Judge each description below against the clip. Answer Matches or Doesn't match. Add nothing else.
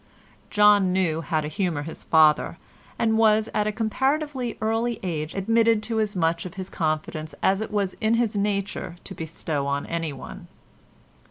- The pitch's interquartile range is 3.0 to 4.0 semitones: Doesn't match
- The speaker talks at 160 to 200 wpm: Matches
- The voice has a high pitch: Matches